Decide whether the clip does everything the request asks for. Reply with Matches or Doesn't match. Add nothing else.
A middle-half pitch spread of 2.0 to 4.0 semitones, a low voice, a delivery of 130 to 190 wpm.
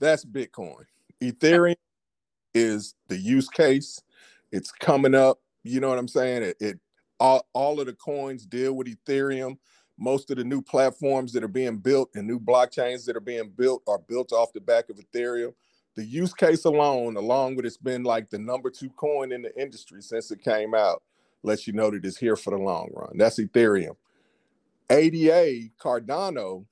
Matches